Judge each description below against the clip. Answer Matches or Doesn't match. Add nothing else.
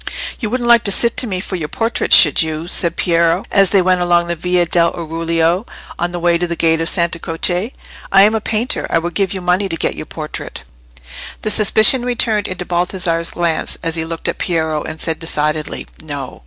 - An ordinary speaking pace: Doesn't match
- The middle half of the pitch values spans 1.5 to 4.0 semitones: Matches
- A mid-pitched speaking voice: Matches